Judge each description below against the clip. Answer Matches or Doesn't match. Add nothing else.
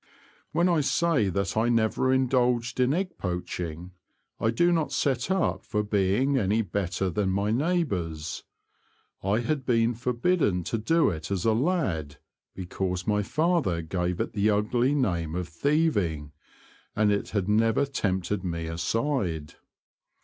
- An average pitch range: Doesn't match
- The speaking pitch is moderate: Doesn't match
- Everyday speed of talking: Matches